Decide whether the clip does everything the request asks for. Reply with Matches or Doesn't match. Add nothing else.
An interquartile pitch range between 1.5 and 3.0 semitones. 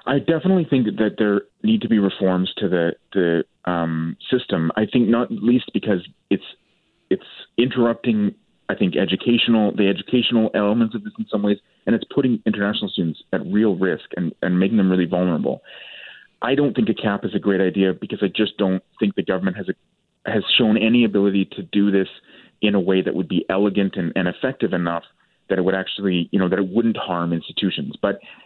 Doesn't match